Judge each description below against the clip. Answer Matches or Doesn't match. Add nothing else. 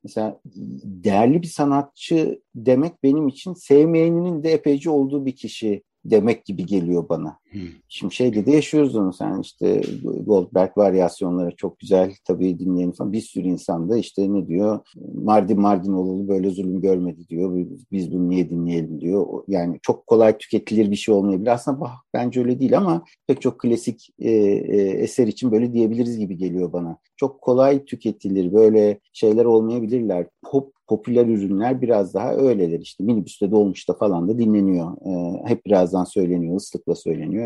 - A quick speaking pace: Matches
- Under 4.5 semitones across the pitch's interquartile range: Doesn't match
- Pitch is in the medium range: Doesn't match